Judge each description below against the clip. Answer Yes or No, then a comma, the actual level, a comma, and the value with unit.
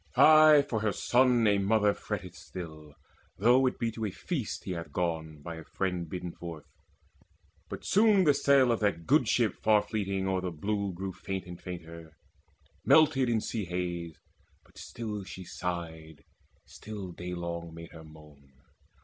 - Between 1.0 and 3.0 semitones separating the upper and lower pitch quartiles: No, average, 4.8 semitones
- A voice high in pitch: No, very low, 95 Hz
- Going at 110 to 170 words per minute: Yes, average, 165 wpm